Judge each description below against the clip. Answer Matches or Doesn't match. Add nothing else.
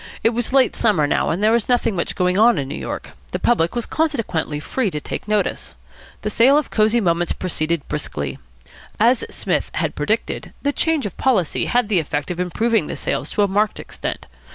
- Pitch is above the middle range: Matches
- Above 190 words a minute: Matches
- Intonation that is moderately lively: Doesn't match